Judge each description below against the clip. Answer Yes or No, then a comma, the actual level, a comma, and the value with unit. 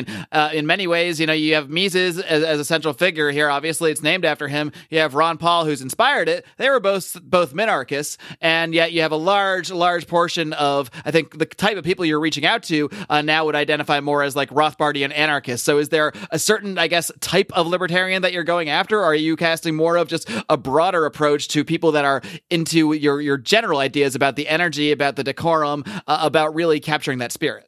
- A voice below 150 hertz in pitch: No, medium, 155 Hz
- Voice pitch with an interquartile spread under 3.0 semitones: Yes, narrow, 2.4 semitones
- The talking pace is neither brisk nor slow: No, fast, 230 wpm